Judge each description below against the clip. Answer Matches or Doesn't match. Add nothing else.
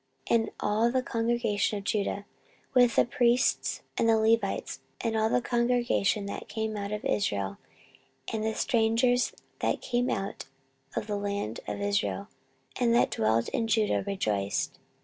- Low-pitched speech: Doesn't match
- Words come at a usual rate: Matches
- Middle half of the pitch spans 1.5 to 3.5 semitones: Matches